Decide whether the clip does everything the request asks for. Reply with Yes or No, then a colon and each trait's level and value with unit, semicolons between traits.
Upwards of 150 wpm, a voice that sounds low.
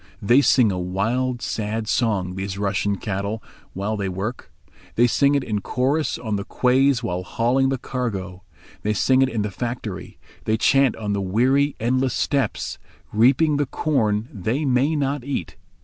Yes: average, 170 wpm; low, 115 Hz